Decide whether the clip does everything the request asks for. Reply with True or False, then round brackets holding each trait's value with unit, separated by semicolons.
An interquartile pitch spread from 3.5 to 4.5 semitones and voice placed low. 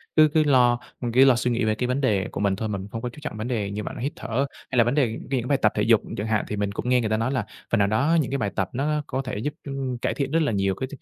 True (4.0 semitones; 120 Hz)